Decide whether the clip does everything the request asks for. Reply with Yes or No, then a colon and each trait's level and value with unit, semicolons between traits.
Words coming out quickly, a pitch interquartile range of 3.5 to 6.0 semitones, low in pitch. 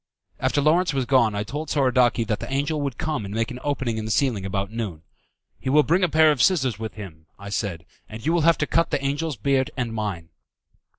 Yes: fast, 235 wpm; wide, 5.6 semitones; low, 125 Hz